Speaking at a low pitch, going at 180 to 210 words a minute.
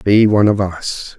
Yes: low, 100 Hz; fast, 205 wpm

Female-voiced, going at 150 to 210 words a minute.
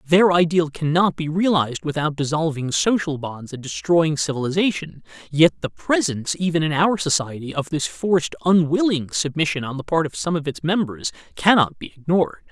No: male; average, 170 wpm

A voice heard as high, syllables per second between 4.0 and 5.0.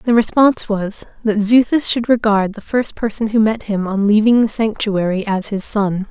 Yes: high, 215 Hz; 4.8 syllables/s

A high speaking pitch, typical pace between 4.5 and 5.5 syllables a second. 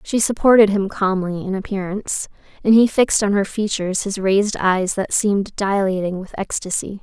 Yes: high, 200 Hz; 5.4 syllables/s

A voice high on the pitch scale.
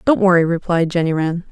No: medium, 175 Hz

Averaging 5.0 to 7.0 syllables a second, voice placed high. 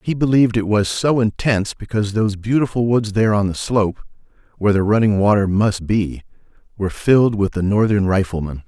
No: 6.0 syllables/s; low, 105 Hz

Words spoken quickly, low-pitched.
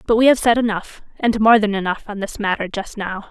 No: fast, 255 wpm; high, 210 Hz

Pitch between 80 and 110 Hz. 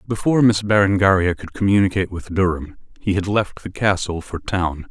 Yes: very low, 95 Hz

